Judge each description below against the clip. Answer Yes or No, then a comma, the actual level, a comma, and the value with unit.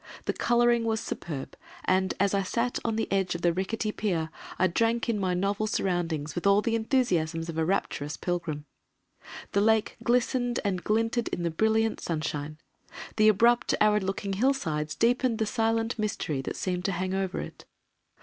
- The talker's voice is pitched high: Yes, high, 200 Hz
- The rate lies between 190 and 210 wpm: No, average, 180 wpm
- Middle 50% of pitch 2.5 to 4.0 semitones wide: No, average, 4.4 semitones